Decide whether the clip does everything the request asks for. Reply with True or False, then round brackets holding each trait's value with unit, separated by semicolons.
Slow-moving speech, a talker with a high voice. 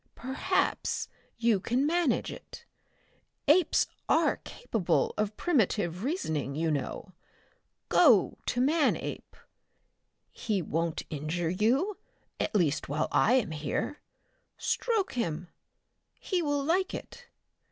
True (110 wpm; 220 Hz)